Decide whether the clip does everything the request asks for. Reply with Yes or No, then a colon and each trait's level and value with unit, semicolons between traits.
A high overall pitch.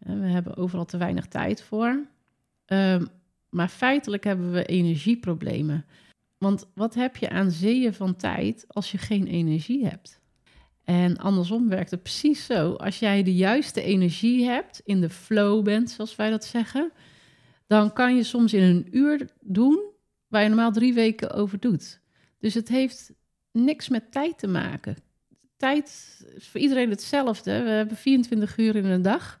Yes: high, 215 Hz